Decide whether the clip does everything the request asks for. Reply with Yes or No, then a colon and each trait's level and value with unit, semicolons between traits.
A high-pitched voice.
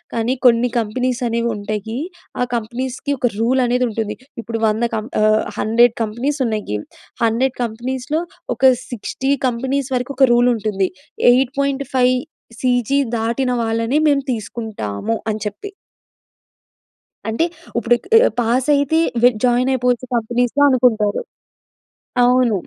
Yes: high, 240 Hz